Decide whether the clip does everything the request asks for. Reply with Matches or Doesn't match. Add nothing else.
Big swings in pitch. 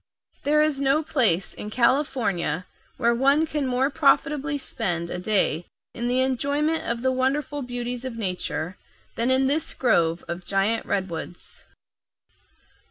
Matches